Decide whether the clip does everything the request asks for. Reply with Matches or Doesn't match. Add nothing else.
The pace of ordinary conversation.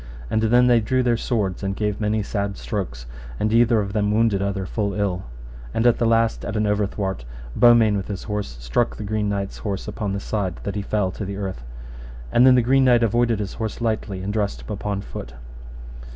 Doesn't match